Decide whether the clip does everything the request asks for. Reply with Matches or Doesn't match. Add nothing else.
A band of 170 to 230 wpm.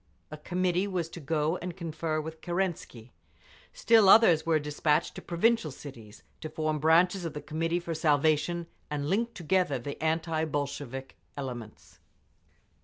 Doesn't match